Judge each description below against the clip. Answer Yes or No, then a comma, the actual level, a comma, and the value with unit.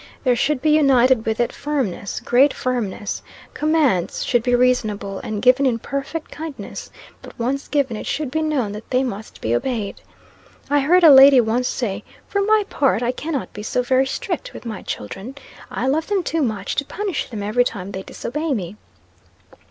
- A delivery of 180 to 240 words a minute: Yes, average, 185 wpm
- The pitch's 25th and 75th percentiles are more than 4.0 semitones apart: Yes, average, 4.9 semitones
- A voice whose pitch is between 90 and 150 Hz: No, very high, 255 Hz